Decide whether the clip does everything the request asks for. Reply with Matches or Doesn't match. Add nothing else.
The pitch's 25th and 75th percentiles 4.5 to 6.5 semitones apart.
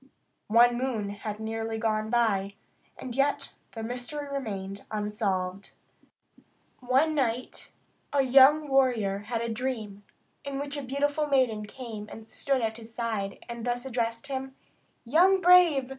Doesn't match